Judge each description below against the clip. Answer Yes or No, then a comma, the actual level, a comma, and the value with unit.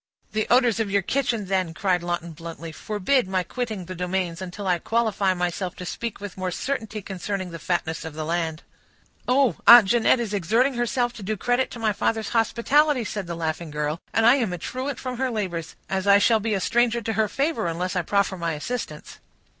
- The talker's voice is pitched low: No, high, 200 Hz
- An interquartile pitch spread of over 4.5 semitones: Yes, average, 5.0 semitones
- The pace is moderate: No, fast, 210 wpm